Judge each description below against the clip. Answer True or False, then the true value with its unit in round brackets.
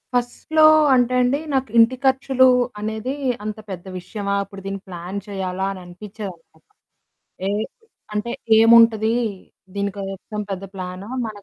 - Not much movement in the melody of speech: False (3.3 semitones)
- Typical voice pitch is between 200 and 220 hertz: True (210 Hz)